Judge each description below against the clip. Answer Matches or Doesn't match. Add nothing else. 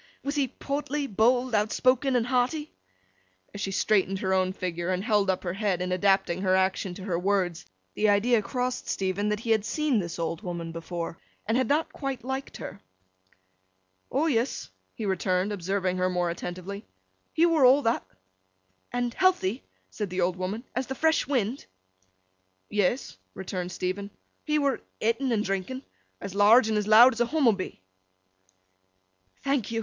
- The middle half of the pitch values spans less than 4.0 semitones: Doesn't match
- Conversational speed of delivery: Matches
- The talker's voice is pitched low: Doesn't match